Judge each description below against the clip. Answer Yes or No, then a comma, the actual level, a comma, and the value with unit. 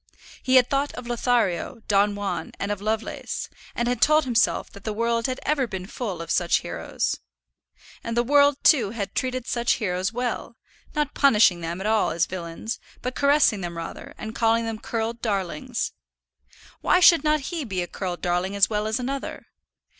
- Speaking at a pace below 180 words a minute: No, average, 185 wpm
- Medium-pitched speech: No, high, 225 Hz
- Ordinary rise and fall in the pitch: Yes, average, 4.4 semitones